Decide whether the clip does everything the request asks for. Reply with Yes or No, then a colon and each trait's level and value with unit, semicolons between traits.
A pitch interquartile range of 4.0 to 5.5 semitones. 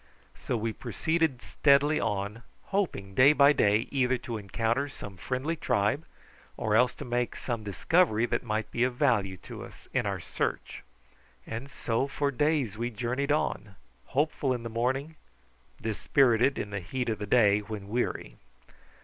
Yes: average, 4.6 semitones